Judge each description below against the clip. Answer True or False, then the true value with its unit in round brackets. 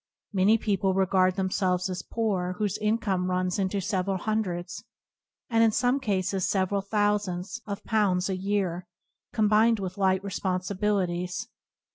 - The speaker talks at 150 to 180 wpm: False (140 wpm)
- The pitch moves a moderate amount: False (2.3 semitones)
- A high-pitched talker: True (195 Hz)